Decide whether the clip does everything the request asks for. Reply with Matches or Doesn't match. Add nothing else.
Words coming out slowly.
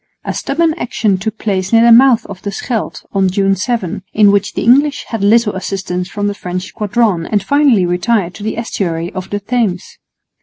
Doesn't match